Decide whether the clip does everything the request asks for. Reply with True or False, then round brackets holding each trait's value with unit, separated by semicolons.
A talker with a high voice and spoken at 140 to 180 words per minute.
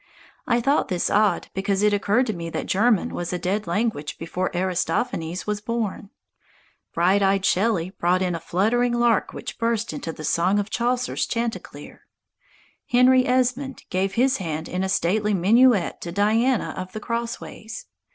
True (205 Hz; 160 wpm)